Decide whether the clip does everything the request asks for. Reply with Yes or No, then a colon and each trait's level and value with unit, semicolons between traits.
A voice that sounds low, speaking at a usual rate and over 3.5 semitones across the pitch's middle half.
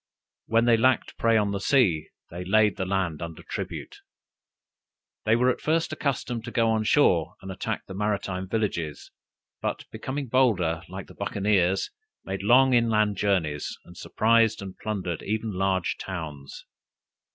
Yes: low, 100 Hz; average, 150 wpm; average, 3.9 semitones